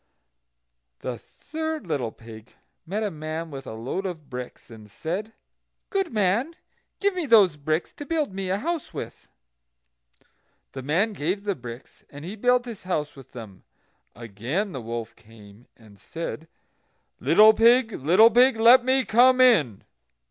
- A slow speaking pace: No, average, 155 wpm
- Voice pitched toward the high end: No, medium, 180 Hz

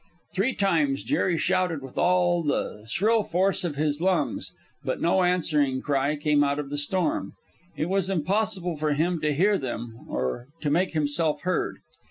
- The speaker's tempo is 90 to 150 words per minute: No, average, 170 wpm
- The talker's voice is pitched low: No, medium, 165 Hz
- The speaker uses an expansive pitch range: No, average, 4.2 semitones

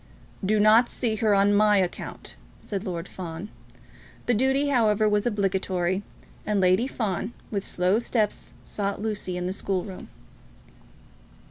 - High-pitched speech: Yes, high, 205 Hz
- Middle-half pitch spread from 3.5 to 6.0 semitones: No, narrow, 2.5 semitones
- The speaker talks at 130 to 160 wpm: Yes, average, 140 wpm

